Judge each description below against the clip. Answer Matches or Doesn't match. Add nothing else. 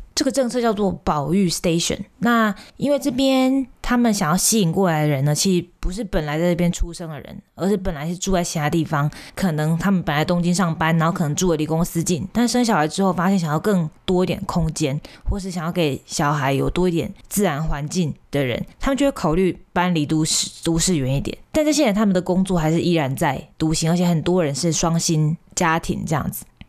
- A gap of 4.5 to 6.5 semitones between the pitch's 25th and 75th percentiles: Doesn't match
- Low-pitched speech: Doesn't match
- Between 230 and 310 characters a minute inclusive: Doesn't match